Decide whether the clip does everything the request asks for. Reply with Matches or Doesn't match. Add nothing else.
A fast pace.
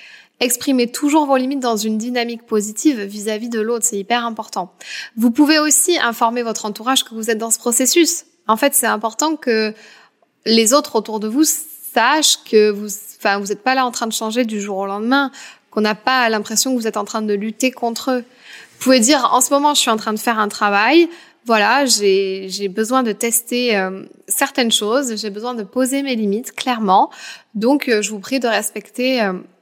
Doesn't match